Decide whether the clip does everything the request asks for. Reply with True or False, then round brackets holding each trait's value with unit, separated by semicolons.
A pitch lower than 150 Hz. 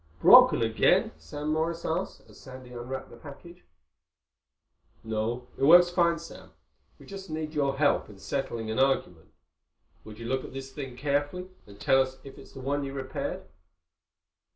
True (135 Hz)